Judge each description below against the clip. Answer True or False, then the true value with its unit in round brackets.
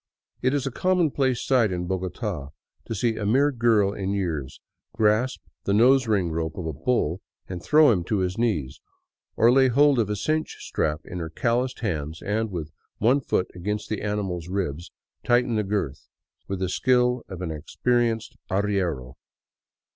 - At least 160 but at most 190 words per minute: True (170 wpm)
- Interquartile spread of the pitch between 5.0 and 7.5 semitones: True (5.5 semitones)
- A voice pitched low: True (105 Hz)